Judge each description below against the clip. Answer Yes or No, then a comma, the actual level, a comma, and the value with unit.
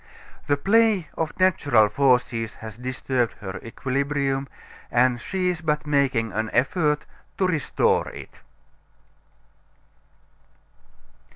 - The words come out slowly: Yes, slow, 100 wpm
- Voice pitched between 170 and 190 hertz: No, low, 135 Hz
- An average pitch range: Yes, average, 4.3 semitones